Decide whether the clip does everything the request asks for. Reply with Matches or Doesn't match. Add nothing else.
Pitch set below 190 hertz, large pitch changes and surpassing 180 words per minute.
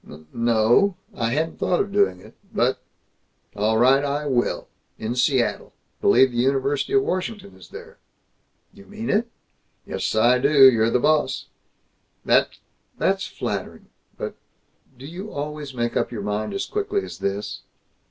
Doesn't match